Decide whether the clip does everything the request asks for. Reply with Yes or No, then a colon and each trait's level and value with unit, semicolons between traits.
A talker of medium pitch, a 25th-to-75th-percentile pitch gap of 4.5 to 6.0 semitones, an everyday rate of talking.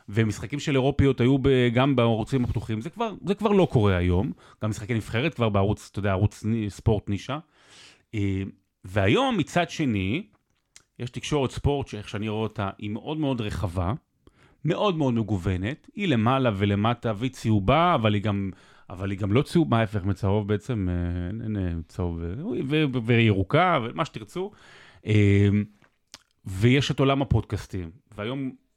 No: low, 110 Hz; average, 4.9 semitones; average, 140 wpm